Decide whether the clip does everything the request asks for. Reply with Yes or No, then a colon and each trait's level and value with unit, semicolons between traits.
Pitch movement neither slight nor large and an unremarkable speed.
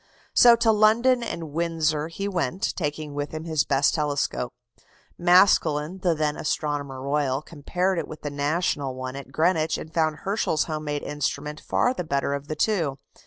Yes: average, 3.4 semitones; average, 170 wpm